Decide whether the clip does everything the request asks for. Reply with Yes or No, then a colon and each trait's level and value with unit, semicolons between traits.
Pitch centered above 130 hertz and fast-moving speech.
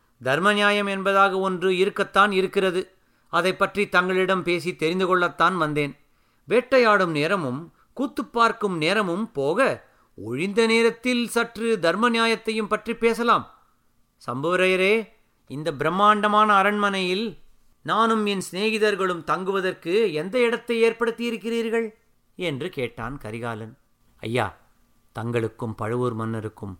No: high, 190 Hz; average, 100 wpm